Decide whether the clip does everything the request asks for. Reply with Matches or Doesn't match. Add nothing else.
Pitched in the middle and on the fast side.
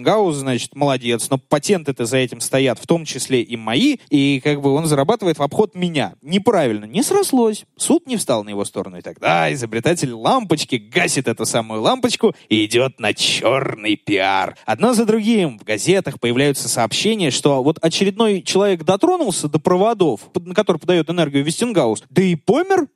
Matches